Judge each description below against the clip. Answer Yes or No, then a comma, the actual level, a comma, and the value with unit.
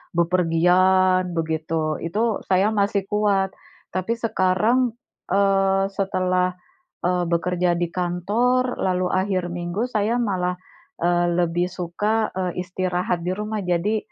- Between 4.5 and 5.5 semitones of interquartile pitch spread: No, narrow, 2.5 semitones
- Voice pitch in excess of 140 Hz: Yes, medium, 185 Hz